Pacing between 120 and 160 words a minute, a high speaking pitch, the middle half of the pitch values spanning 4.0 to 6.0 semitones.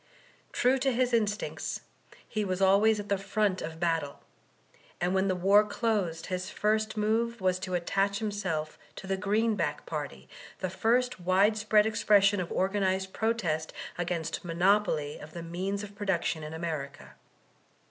No: average, 150 wpm; high, 195 Hz; average, 3.3 semitones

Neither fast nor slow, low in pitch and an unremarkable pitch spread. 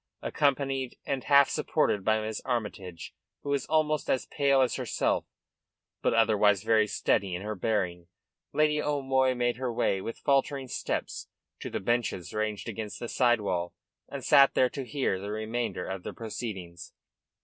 Yes: average, 160 wpm; low, 115 Hz; average, 4.7 semitones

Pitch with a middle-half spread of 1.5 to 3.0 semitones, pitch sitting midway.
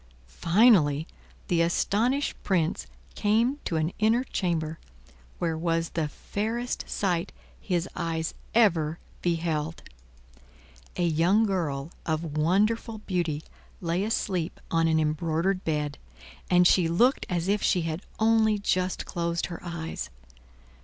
No: average, 4.0 semitones; medium, 170 Hz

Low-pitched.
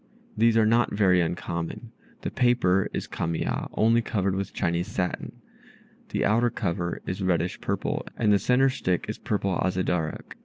Yes: very low, 95 Hz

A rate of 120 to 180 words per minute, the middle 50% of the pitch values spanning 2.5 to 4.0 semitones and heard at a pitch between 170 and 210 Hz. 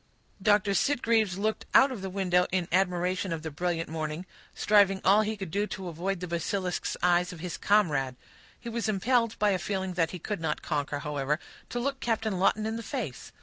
No: average, 195 wpm; average, 3.7 semitones; high, 190 Hz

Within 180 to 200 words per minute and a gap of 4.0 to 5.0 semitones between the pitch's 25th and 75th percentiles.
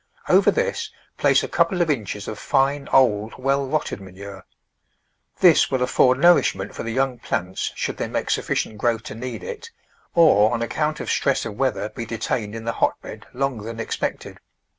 Yes: average, 185 wpm; average, 4.4 semitones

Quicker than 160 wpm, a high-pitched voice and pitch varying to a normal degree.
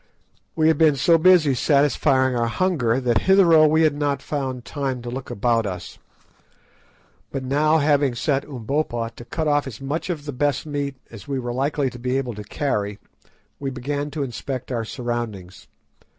No: average, 180 wpm; low, 135 Hz; average, 3.4 semitones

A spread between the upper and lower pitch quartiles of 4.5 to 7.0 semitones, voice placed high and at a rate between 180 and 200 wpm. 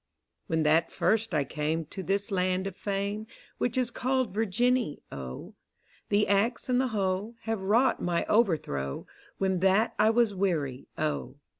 No: average, 5.2 semitones; high, 195 Hz; average, 155 wpm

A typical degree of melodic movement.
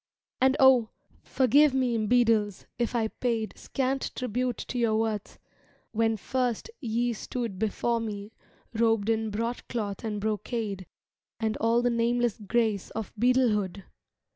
No: narrow, 2.2 semitones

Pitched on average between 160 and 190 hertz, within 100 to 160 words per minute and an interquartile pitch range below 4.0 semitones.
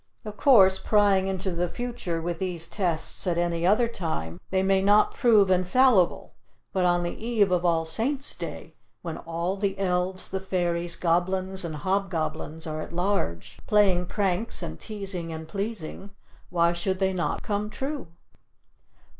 Yes: medium, 185 Hz; average, 155 wpm; average, 2.9 semitones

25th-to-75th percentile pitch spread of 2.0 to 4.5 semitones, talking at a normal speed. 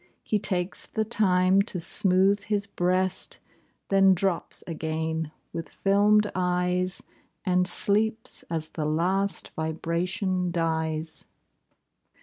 No: average, 3.0 semitones; slow, 105 wpm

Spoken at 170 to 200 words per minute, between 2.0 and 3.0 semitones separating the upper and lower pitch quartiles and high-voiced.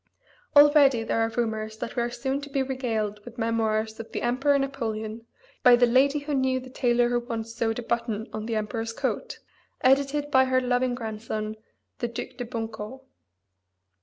Yes: average, 180 wpm; average, 2.7 semitones; high, 240 Hz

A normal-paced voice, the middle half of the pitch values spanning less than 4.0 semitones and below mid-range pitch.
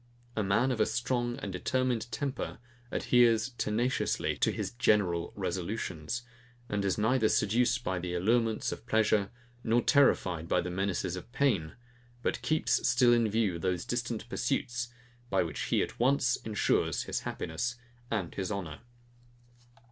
No: average, 150 wpm; average, 4.5 semitones; low, 110 Hz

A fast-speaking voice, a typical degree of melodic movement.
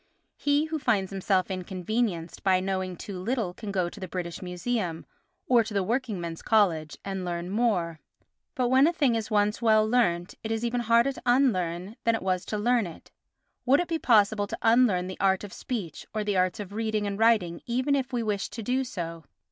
Yes: fast, 210 wpm; average, 4.5 semitones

